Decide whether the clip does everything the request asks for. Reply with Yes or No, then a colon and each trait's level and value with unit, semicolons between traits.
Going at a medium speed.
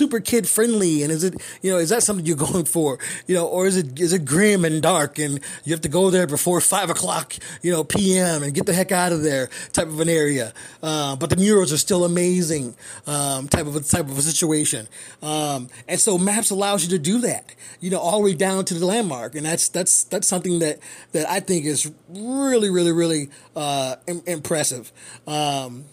No: fast, 220 wpm